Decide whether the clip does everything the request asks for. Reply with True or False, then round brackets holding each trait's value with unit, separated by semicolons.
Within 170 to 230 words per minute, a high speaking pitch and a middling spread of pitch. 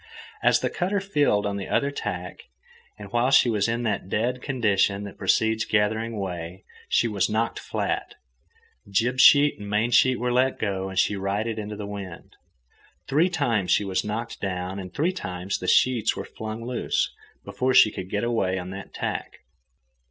False (180 wpm; 105 Hz; 3.9 semitones)